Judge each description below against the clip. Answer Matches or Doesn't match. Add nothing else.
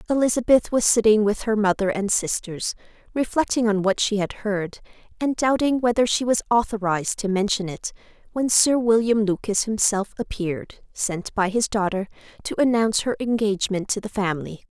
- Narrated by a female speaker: Matches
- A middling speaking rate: Matches